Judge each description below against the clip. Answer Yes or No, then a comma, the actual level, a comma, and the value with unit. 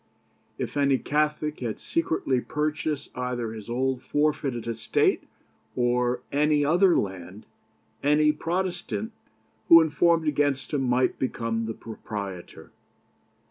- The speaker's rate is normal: No, slow, 110 wpm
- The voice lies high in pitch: No, medium, 140 Hz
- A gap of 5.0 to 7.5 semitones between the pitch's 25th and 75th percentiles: No, average, 4.1 semitones